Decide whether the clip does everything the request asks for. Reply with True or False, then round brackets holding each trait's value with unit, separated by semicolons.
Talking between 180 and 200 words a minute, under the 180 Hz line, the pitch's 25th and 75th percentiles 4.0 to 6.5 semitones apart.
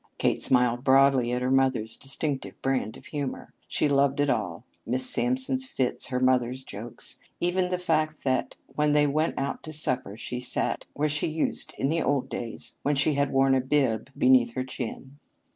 False (185 wpm; 135 Hz; 2.8 semitones)